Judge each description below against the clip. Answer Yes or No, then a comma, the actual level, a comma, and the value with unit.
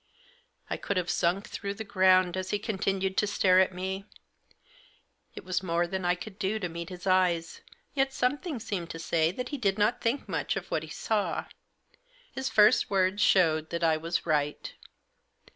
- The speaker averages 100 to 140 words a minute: No, average, 185 wpm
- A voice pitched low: No, medium, 185 Hz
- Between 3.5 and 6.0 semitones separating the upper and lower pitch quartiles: No, average, 3.0 semitones